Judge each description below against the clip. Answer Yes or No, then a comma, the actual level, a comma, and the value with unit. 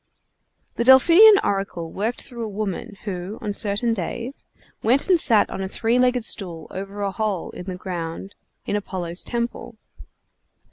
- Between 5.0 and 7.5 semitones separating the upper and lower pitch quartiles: No, average, 3.9 semitones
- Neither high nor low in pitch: No, high, 205 Hz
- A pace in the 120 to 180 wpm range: Yes, average, 155 wpm